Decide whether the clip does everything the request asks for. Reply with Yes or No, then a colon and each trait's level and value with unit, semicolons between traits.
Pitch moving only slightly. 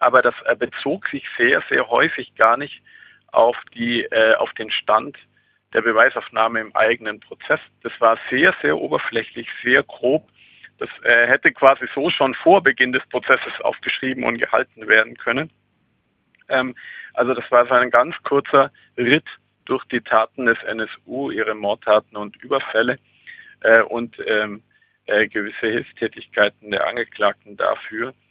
Yes: narrow, 2.1 semitones